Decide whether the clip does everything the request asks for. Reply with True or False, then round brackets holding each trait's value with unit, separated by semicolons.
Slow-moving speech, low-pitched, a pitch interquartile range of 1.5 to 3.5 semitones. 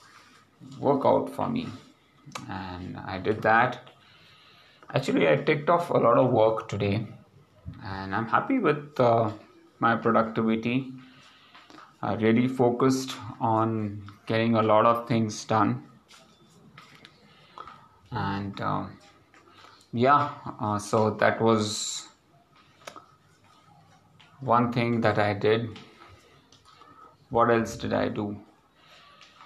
True (100 wpm; 115 Hz; 3.2 semitones)